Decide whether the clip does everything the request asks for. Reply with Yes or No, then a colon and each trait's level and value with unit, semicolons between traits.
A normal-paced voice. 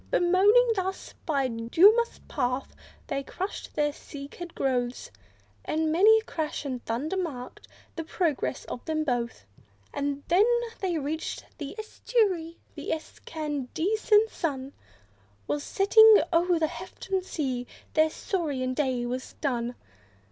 No: slow, 125 wpm